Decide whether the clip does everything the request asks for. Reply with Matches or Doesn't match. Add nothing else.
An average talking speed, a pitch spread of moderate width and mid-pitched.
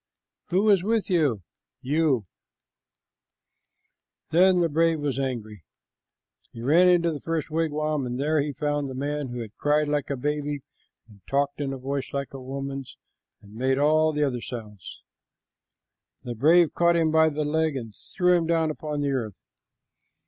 Matches